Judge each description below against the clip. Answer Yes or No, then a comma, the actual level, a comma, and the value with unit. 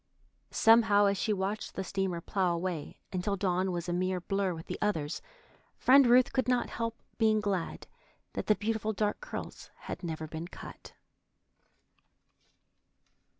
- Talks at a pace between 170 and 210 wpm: No, average, 150 wpm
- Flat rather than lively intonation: No, average, 3.4 semitones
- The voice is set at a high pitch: Yes, high, 195 Hz